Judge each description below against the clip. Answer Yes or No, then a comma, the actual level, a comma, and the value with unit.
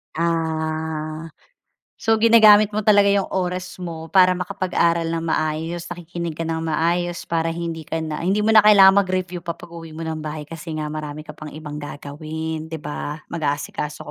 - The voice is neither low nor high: Yes, medium, 165 Hz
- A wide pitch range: No, narrow, 2.5 semitones